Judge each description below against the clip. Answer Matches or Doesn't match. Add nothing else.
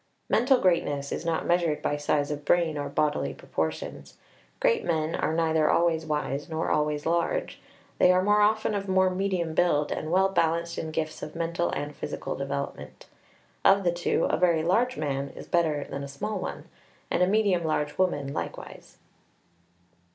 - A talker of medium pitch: Matches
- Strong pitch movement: Doesn't match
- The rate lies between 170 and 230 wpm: Matches